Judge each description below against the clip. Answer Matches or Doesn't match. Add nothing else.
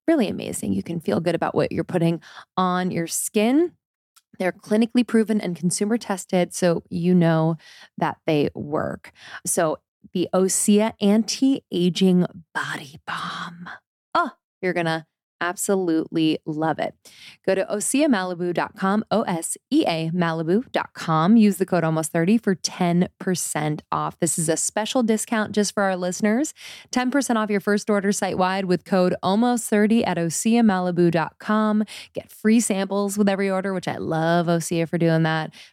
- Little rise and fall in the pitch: Doesn't match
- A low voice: Doesn't match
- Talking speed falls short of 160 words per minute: Matches